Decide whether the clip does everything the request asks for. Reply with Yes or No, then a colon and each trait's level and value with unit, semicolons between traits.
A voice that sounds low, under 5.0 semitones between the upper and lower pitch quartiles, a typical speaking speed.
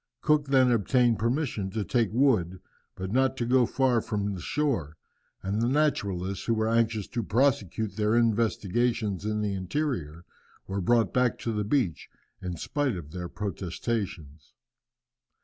Yes: low, 110 Hz; average, 4.5 semitones; average, 150 wpm